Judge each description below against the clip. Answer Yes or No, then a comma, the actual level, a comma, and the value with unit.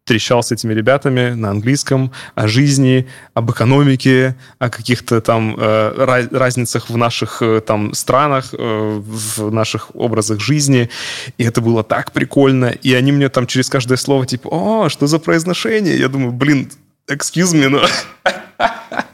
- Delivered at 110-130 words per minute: No, average, 150 wpm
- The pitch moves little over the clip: No, average, 3.0 semitones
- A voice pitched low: Yes, low, 125 Hz